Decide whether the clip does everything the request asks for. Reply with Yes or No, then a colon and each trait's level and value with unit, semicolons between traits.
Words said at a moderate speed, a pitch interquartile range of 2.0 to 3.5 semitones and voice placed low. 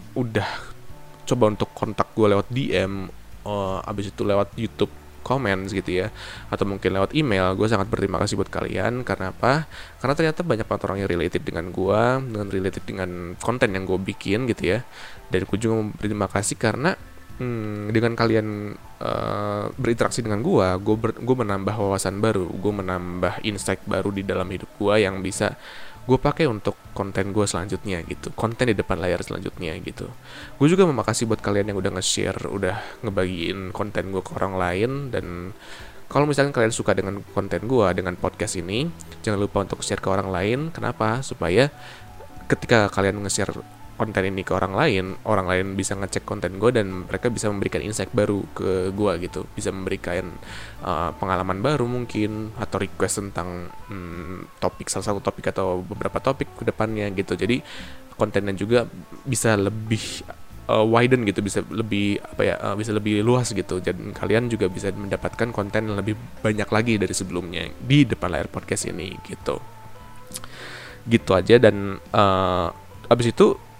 No: fast, 170 wpm; average, 2.8 semitones; low, 100 Hz